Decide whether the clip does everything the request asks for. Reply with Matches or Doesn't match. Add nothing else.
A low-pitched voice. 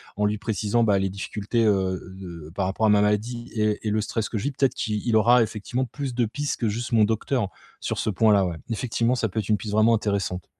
Matches